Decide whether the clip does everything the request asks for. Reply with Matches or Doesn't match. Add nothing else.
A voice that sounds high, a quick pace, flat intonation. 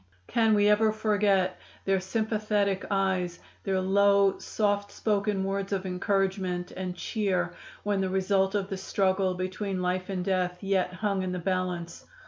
Doesn't match